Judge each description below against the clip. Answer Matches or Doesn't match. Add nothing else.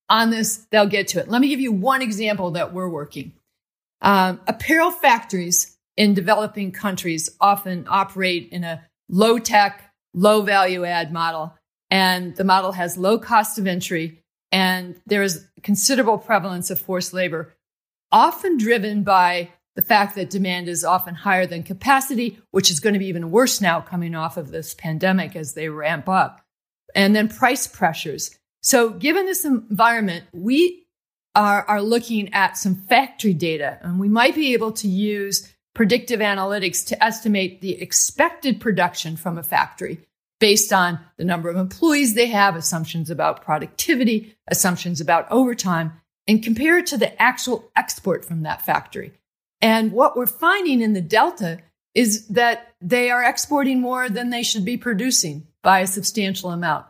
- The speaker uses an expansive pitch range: Doesn't match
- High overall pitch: Matches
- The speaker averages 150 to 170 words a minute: Matches